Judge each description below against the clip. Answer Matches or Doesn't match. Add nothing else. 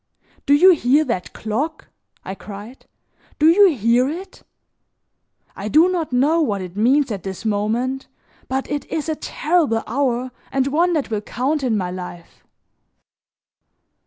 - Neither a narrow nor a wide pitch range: Doesn't match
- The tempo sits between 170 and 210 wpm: Doesn't match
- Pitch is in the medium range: Doesn't match